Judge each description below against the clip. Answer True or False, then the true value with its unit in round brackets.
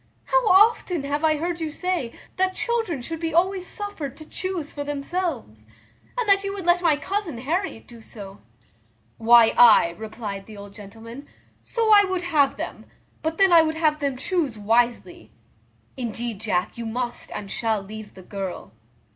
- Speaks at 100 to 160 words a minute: False (170 wpm)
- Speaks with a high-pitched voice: True (290 Hz)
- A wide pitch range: True (8.1 semitones)